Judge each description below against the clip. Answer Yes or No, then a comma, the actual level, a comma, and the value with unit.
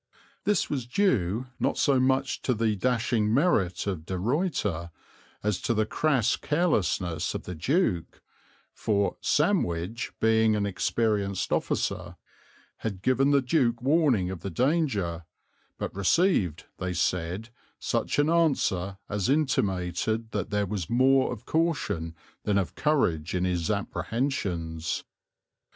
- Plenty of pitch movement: Yes, wide, 6.7 semitones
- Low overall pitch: Yes, low, 110 Hz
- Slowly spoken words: Yes, slow, 130 wpm